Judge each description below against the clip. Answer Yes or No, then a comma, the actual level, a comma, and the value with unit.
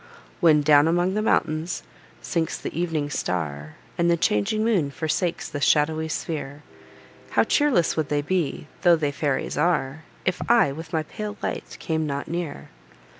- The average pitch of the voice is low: No, medium, 160 Hz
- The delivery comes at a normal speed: Yes, average, 160 wpm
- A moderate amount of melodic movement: Yes, average, 3.3 semitones